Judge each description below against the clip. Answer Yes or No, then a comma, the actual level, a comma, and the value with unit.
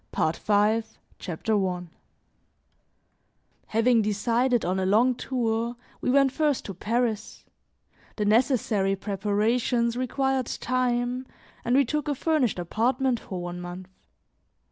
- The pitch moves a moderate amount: Yes, average, 3.8 semitones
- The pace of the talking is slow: Yes, slow, 120 wpm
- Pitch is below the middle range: No, high, 230 Hz